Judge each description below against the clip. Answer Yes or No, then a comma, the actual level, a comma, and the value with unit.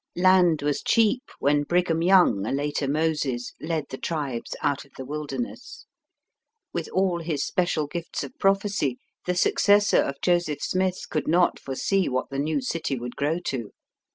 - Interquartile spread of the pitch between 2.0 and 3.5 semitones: No, average, 4.4 semitones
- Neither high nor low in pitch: Yes, medium, 160 Hz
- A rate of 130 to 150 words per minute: No, average, 160 wpm